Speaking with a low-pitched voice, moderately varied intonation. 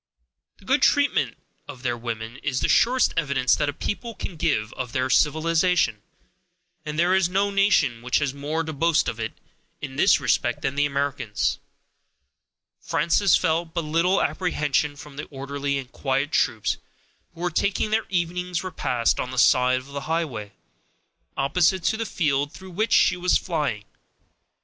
No: medium, 150 Hz; average, 5.0 semitones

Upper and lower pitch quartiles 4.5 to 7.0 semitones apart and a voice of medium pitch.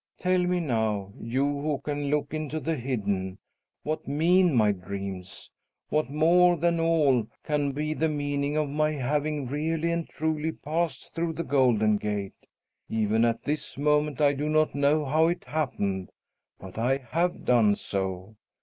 Yes: average, 5.2 semitones; medium, 145 Hz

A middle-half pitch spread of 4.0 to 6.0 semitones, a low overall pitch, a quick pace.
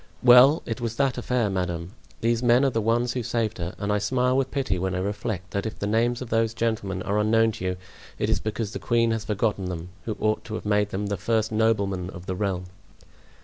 No: average, 3.1 semitones; low, 110 Hz; fast, 235 wpm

